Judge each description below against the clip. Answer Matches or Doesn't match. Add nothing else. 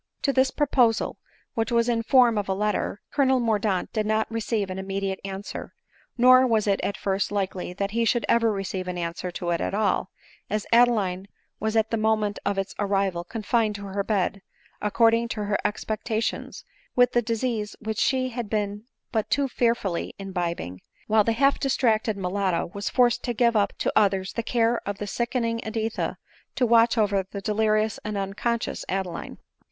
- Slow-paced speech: Doesn't match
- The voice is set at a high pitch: Matches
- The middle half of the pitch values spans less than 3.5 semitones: Matches